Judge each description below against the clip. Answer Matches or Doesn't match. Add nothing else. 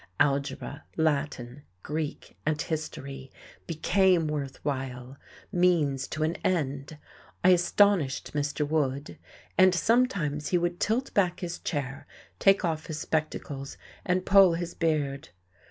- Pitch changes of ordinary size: Matches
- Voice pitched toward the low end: Doesn't match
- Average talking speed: Doesn't match